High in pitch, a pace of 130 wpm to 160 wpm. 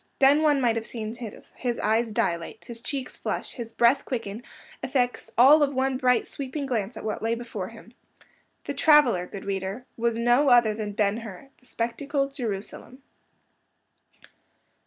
Yes: high, 240 Hz; average, 155 wpm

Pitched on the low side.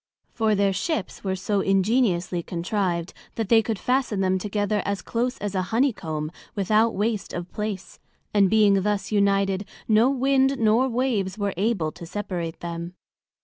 No: high, 205 Hz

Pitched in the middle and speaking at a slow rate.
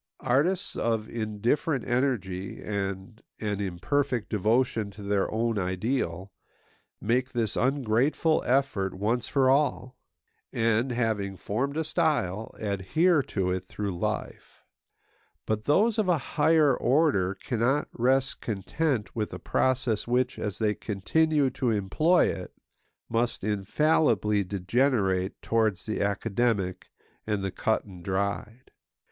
No: low, 115 Hz; slow, 120 wpm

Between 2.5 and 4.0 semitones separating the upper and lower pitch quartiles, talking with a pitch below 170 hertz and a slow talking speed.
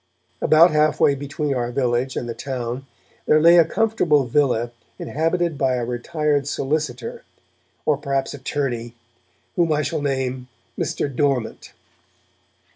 Yes: average, 3.3 semitones; medium, 140 Hz; slow, 130 wpm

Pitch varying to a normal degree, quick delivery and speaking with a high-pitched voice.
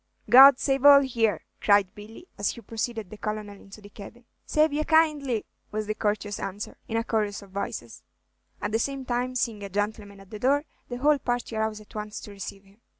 Yes: average, 3.7 semitones; fast, 210 wpm; high, 220 Hz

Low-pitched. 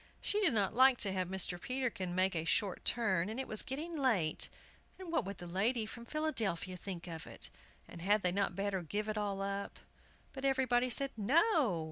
No: high, 205 Hz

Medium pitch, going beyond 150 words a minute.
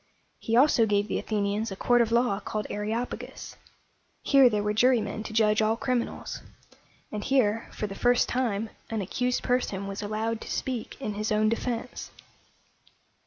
No: high, 220 Hz; average, 175 wpm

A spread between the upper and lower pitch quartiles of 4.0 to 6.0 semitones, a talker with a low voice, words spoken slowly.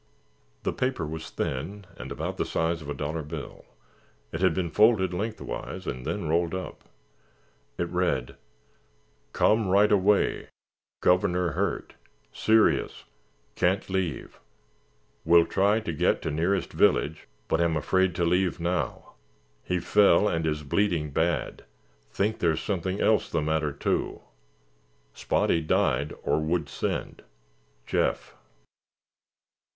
No: average, 3.3 semitones; very low, 85 Hz; slow, 125 wpm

